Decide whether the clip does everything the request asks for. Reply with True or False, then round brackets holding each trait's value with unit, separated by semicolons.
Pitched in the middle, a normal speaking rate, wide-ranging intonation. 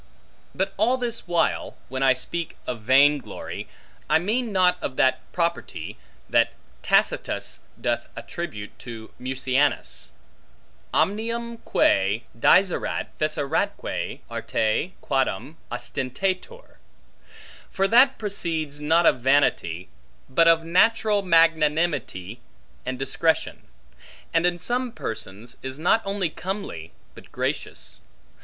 False (165 Hz; 110 wpm; 6.8 semitones)